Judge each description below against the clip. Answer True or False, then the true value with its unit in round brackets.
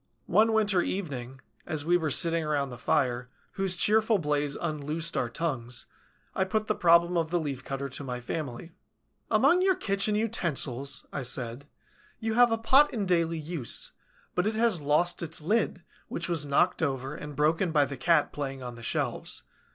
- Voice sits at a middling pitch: True (160 Hz)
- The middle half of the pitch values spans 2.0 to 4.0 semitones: False (5.4 semitones)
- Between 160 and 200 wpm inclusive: True (180 wpm)